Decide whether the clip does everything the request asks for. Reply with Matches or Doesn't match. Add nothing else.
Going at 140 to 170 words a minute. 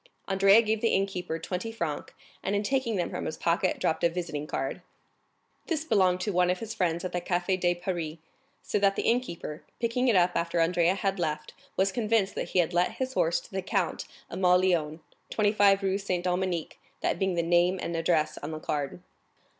Doesn't match